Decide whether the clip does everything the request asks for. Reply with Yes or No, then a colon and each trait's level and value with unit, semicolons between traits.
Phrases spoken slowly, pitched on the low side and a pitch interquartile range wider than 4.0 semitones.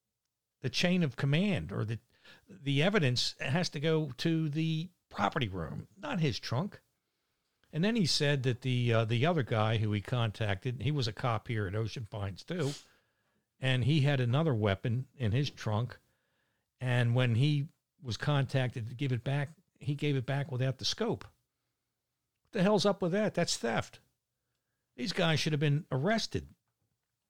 No: average, 170 wpm; low, 130 Hz; average, 4.7 semitones